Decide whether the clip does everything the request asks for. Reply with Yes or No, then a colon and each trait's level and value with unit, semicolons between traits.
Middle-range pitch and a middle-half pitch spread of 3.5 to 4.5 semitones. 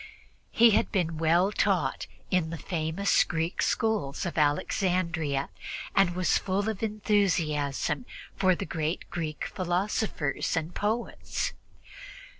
Yes: medium, 175 Hz; average, 3.9 semitones